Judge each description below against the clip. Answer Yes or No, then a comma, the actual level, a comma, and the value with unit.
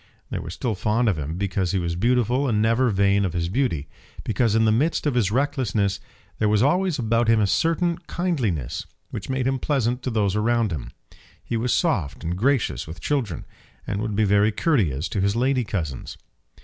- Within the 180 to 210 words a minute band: Yes, average, 200 wpm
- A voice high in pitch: No, low, 110 Hz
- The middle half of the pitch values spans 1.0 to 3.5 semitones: No, average, 4.6 semitones